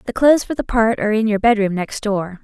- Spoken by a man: No, female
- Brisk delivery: Yes, fast, 270 wpm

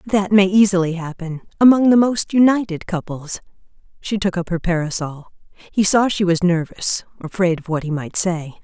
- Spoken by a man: No, female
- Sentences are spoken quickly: No, average, 175 wpm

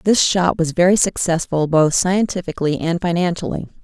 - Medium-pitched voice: Yes, medium, 175 Hz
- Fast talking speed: No, average, 140 wpm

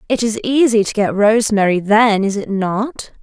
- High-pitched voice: Yes, high, 215 Hz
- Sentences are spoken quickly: No, average, 185 wpm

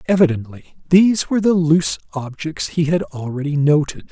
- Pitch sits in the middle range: Yes, medium, 155 Hz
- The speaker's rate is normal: Yes, average, 145 wpm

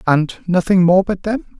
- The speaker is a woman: No, male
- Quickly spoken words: No, average, 190 wpm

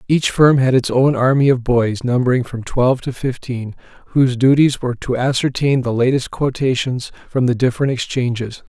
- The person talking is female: No, male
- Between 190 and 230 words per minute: No, average, 170 wpm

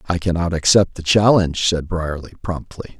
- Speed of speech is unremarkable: Yes, average, 160 wpm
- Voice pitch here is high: No, very low, 85 Hz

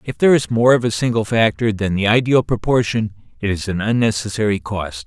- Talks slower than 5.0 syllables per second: No, 5.7 syllables/s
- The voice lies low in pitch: Yes, low, 110 Hz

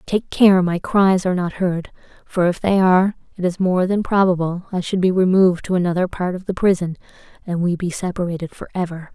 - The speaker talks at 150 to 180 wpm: No, fast, 205 wpm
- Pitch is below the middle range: No, medium, 180 Hz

